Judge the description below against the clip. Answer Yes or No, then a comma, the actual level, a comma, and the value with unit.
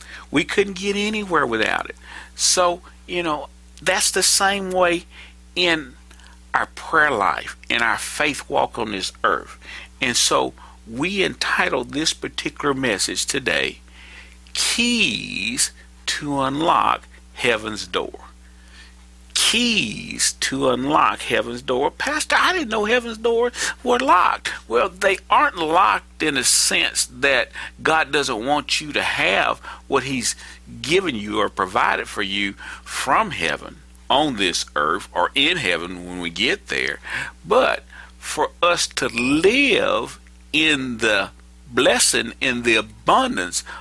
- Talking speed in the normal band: No, slow, 130 wpm